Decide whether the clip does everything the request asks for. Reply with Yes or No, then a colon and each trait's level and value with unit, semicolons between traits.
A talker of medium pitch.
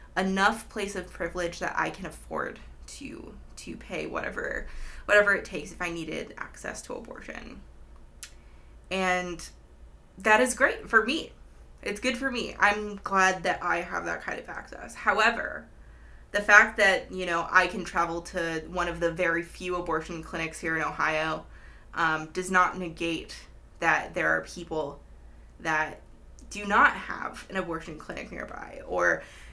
Yes: medium, 175 Hz